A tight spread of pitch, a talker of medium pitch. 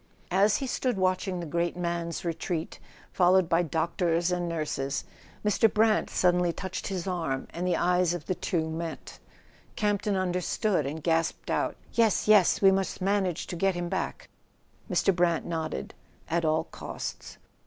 Yes: narrow, 2.3 semitones; medium, 175 Hz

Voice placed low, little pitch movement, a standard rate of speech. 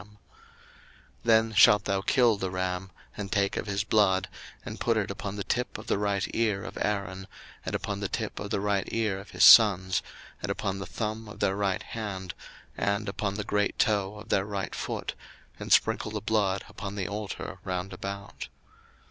Yes: low, 100 Hz; narrow, 1.5 semitones; average, 190 wpm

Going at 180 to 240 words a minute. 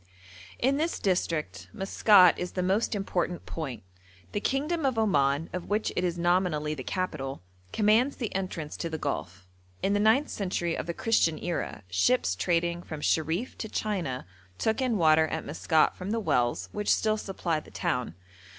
No: average, 170 wpm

